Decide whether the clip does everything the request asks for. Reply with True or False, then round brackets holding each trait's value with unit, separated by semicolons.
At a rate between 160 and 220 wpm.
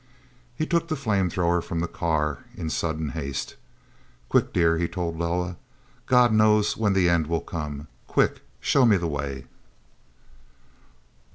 False (150 wpm)